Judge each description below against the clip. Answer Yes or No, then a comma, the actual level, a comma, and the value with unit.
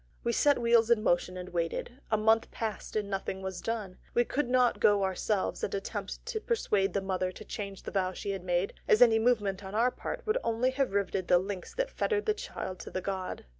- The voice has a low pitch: No, high, 205 Hz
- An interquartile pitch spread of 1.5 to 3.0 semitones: No, average, 3.9 semitones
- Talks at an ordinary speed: No, fast, 225 wpm